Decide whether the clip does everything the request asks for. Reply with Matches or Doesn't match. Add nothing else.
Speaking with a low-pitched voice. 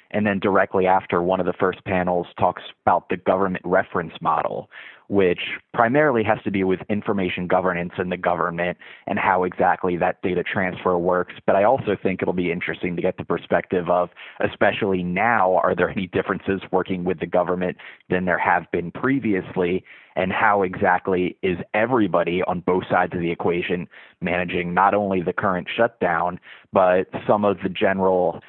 Matches